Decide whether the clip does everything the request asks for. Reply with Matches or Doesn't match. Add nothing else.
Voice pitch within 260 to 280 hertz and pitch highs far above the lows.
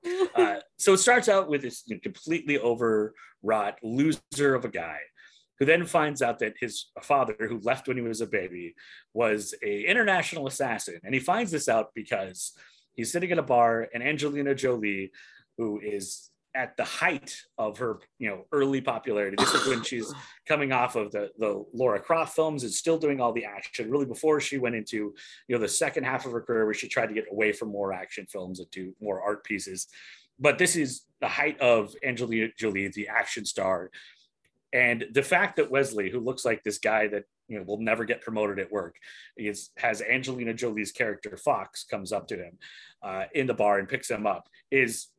Doesn't match